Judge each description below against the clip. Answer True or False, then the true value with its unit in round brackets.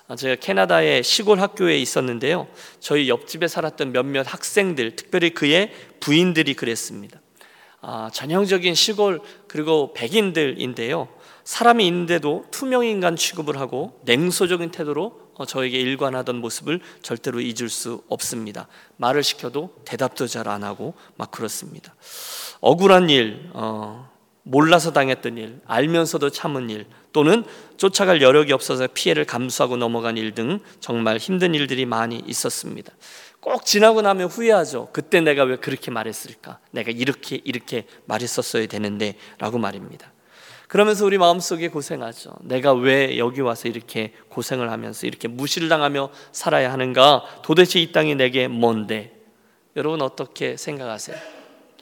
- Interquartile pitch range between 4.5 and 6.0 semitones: False (6.5 semitones)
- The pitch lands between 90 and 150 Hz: True (140 Hz)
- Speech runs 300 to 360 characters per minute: True (330 characters per minute)